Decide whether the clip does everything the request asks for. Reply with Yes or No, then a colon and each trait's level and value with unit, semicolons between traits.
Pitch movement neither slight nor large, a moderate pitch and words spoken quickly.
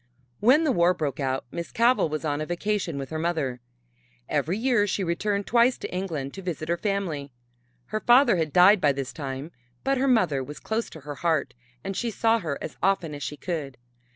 No: wide, 6.1 semitones; medium, 170 Hz; fast, 210 wpm